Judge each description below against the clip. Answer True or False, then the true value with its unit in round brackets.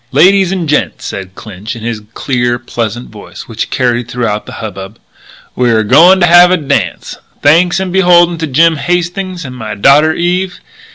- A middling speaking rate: True (175 wpm)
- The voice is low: False (145 Hz)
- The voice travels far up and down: True (7.1 semitones)